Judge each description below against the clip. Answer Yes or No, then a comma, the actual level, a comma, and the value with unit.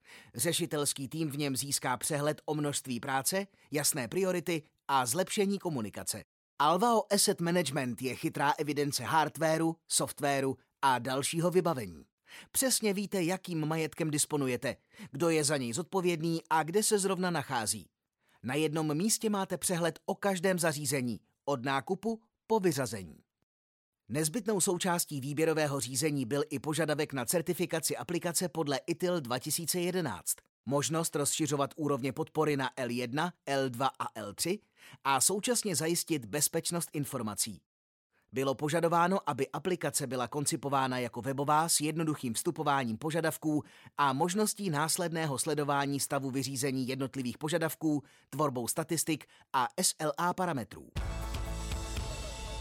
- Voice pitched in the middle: Yes, medium, 150 Hz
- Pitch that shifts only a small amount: No, average, 4.2 semitones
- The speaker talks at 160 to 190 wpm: No, average, 120 wpm